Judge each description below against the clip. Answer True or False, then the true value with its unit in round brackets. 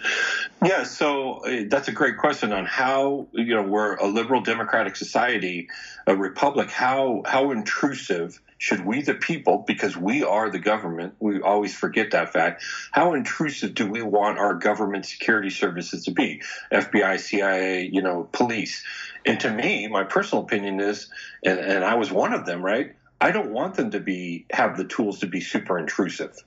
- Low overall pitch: True (105 Hz)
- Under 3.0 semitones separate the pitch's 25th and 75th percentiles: False (3.8 semitones)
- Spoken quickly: False (180 wpm)